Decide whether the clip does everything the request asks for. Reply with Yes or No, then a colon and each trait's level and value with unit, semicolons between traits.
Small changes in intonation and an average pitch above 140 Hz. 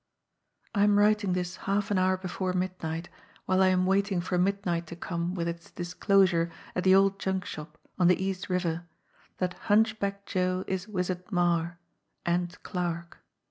Yes: narrow, 1.9 semitones; medium, 185 Hz